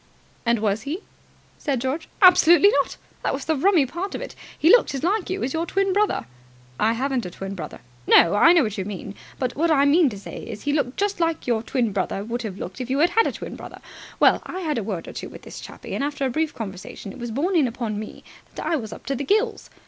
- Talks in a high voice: Yes, very high, 270 Hz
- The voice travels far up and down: Yes, wide, 7.2 semitones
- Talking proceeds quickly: Yes, fast, 260 wpm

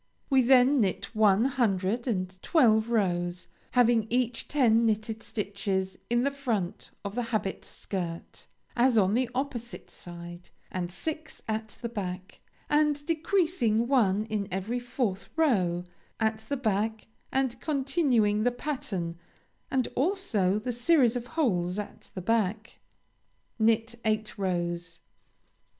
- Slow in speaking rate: Yes, slow, 130 wpm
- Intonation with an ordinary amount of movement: Yes, average, 4.7 semitones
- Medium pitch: No, high, 220 Hz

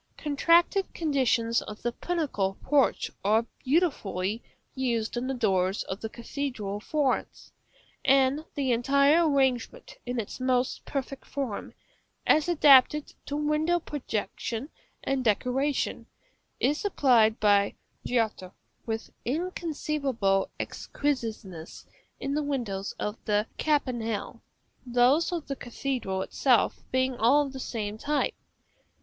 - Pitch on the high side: Yes, very high, 255 Hz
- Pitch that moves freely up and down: No, average, 4.6 semitones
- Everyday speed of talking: No, slow, 120 wpm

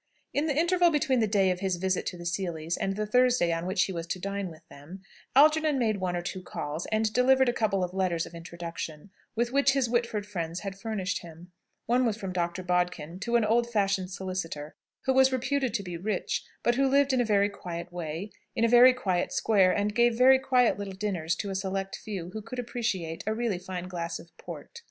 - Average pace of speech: No, fast, 225 wpm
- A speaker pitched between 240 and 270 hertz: No, high, 195 Hz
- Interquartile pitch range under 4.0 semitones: No, average, 5.2 semitones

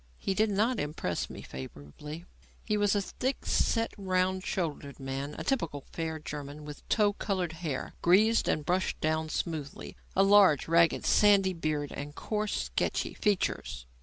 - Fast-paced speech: No, average, 155 wpm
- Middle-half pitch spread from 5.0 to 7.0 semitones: Yes, average, 5.3 semitones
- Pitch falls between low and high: Yes, medium, 170 Hz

